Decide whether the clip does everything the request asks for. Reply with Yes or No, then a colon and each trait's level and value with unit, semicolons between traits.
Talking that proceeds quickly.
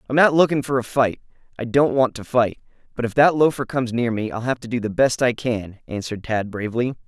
Yes: fast, 235 wpm